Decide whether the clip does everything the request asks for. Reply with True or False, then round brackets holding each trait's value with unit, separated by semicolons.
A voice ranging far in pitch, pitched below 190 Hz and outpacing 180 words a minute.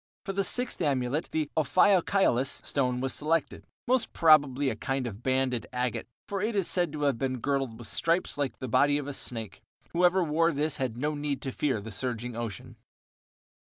False (4.4 semitones; 140 Hz; 190 wpm)